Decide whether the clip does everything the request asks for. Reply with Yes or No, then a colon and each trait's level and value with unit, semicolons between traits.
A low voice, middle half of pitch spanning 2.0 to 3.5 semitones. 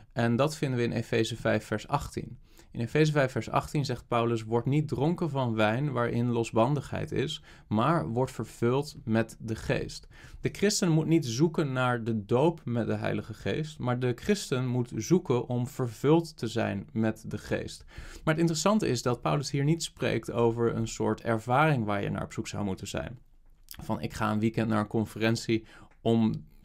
No: low, 120 Hz; average, 4.3 semitones